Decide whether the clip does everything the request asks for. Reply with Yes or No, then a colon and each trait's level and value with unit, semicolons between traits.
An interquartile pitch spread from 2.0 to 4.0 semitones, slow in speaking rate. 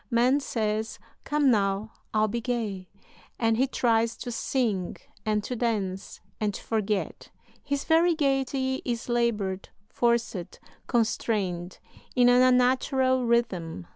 Yes: average, 3.3 semitones; slow, 125 wpm